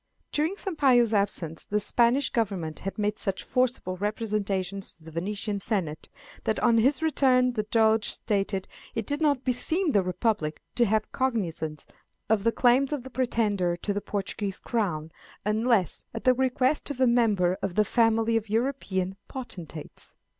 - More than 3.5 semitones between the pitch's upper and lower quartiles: Yes, average, 4.4 semitones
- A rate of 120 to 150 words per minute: No, average, 160 wpm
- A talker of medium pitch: No, high, 220 Hz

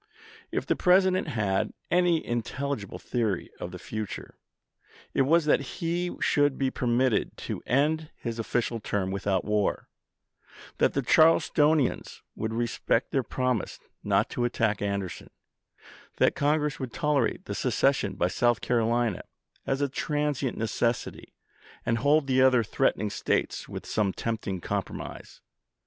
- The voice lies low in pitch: Yes, low, 125 Hz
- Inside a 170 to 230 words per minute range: No, average, 140 wpm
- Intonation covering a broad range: No, average, 4.9 semitones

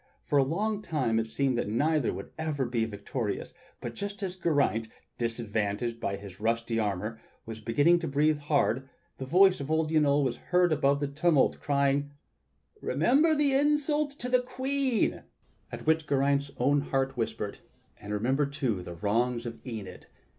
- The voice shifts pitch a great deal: Yes, wide, 5.9 semitones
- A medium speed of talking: Yes, average, 160 wpm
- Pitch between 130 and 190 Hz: Yes, medium, 140 Hz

